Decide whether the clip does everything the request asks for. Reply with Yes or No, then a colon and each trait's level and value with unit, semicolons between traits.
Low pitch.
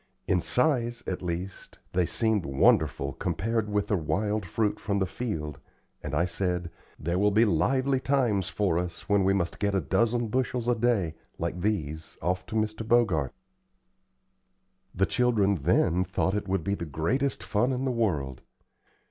Yes: low, 100 Hz